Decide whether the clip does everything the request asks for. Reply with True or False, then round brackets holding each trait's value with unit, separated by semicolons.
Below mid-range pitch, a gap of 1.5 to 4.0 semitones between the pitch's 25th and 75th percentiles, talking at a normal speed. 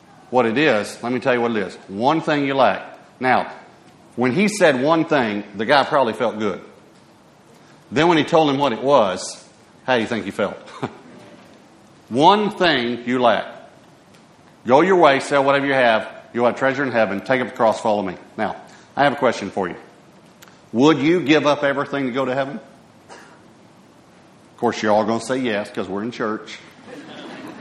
True (130 Hz; 3.3 semitones; 195 wpm)